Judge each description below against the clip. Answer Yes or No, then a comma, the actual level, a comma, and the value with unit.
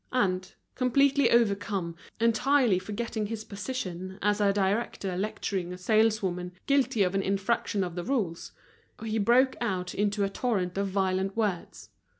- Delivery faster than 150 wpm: No, average, 145 wpm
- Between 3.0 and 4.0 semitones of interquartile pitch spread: Yes, average, 3.7 semitones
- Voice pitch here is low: No, high, 200 Hz